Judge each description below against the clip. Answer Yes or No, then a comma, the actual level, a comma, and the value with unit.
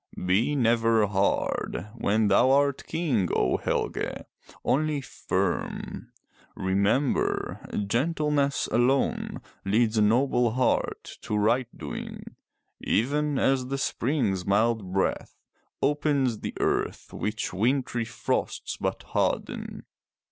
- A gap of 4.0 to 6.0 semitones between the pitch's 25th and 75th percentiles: Yes, average, 4.7 semitones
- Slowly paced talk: Yes, slow, 105 wpm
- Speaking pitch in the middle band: No, low, 120 Hz